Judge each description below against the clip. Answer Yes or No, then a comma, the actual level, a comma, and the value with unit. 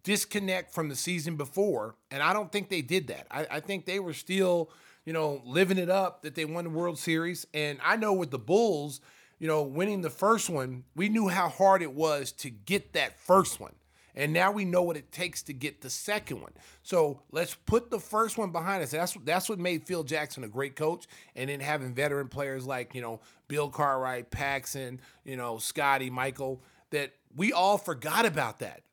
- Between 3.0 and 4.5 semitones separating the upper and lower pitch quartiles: No, average, 5.3 semitones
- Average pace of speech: No, fast, 210 wpm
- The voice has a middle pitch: Yes, medium, 155 Hz